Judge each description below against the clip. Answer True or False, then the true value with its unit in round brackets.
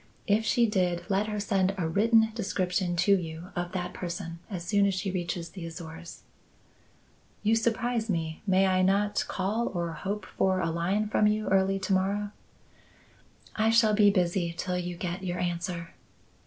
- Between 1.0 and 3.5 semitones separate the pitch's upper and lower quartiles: True (2.9 semitones)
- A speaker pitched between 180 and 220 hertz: True (190 Hz)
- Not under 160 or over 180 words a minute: True (170 wpm)